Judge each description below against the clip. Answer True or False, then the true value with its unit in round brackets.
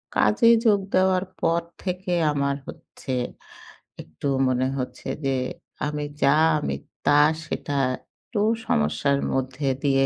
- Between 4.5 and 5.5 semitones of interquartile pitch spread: True (5.0 semitones)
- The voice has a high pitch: False (140 Hz)